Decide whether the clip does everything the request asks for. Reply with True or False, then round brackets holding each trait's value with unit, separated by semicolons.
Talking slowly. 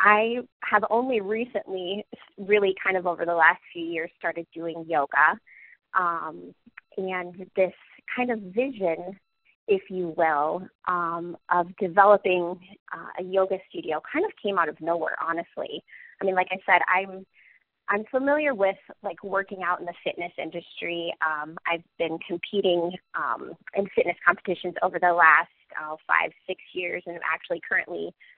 False (155 wpm)